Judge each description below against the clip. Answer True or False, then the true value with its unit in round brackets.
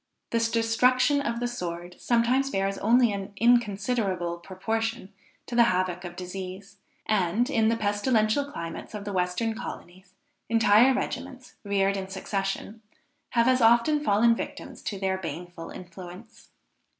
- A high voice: True (205 Hz)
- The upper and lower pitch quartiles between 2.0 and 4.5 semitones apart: True (3.9 semitones)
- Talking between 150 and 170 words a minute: False (140 wpm)